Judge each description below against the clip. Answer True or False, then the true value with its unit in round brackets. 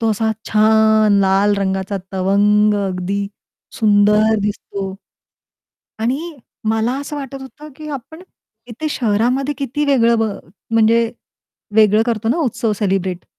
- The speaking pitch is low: False (220 Hz)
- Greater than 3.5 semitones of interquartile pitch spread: False (3.1 semitones)